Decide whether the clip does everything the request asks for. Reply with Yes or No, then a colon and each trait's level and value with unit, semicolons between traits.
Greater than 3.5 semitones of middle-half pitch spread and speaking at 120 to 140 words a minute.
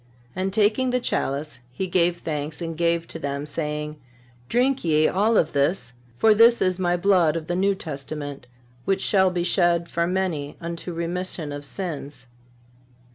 No: average, 4.0 semitones; average, 165 wpm